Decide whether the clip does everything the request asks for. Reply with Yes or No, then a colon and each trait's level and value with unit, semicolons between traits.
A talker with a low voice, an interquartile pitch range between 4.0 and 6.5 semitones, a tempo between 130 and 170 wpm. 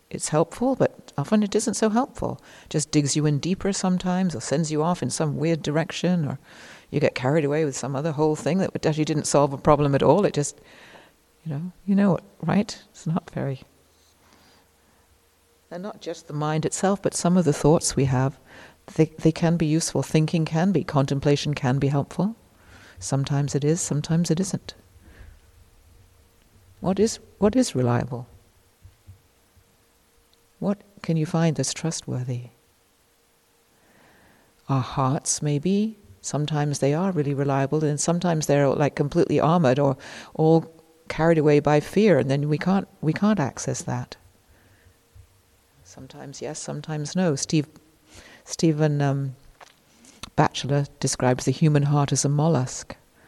No: medium, 145 Hz; average, 4.8 semitones; average, 155 wpm